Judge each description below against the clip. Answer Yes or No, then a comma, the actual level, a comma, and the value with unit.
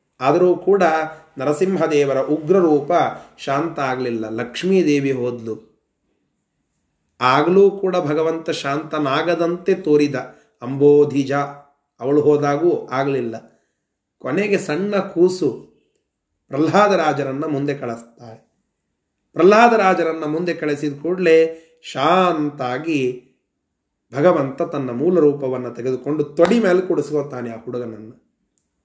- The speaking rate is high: No, average, 80 wpm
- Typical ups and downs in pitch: Yes, average, 4.6 semitones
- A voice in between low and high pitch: Yes, medium, 145 Hz